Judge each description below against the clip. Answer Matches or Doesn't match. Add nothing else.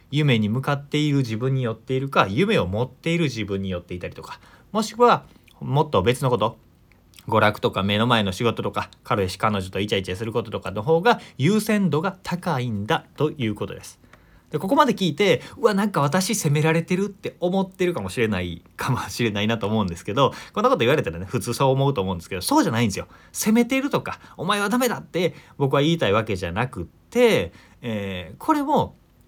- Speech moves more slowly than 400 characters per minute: Doesn't match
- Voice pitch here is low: Matches